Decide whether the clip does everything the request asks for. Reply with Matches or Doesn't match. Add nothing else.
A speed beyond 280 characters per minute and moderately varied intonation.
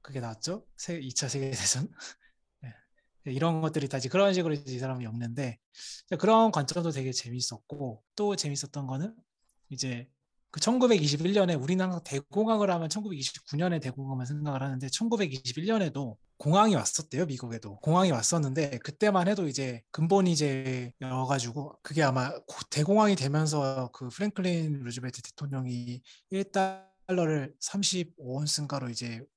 Doesn't match